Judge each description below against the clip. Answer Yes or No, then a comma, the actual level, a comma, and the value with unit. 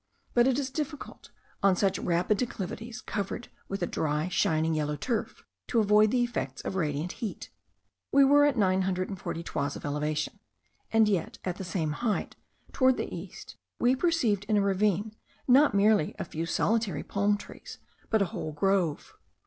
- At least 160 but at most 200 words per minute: Yes, average, 175 wpm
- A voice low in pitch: No, high, 200 Hz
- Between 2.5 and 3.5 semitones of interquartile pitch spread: No, average, 5.2 semitones